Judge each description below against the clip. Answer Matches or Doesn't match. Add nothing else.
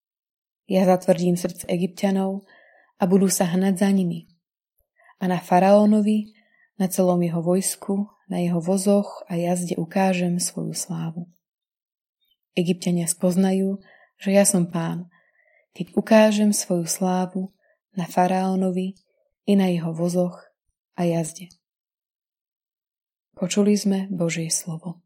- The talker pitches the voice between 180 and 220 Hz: Matches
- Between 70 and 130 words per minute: Matches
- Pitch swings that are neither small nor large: Doesn't match